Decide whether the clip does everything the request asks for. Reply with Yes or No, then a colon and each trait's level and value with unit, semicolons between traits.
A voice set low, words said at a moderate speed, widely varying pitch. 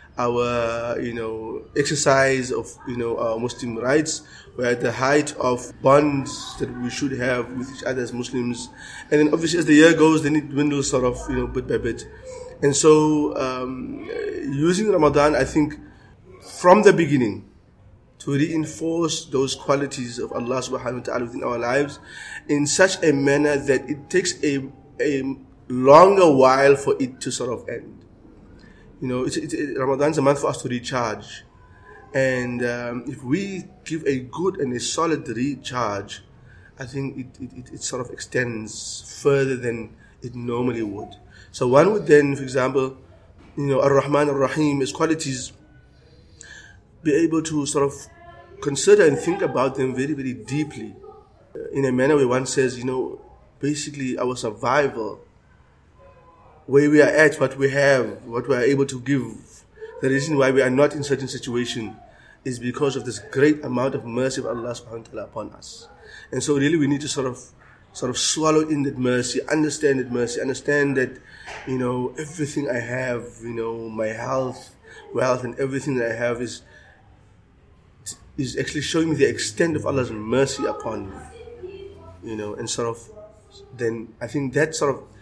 No: low, 130 Hz; average, 170 wpm; average, 3.2 semitones